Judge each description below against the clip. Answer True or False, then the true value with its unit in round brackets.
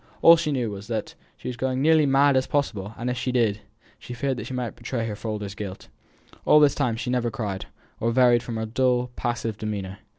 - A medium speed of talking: False (230 wpm)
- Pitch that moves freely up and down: False (3.2 semitones)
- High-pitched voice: False (120 Hz)